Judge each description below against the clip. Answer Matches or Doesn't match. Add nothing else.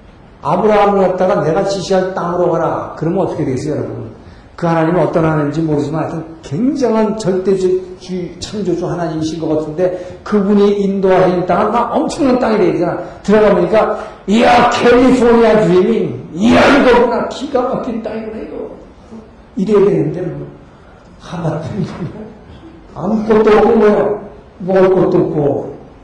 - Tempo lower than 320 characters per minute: Doesn't match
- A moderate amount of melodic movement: Matches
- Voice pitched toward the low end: Doesn't match